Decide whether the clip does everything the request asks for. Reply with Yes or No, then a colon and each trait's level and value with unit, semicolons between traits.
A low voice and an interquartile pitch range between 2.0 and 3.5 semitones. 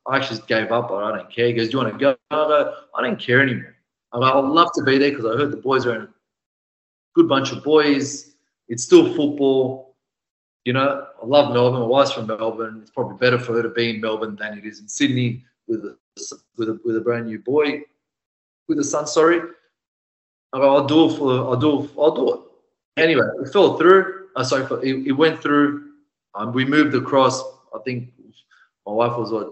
No: low, 130 Hz; average, 4.0 semitones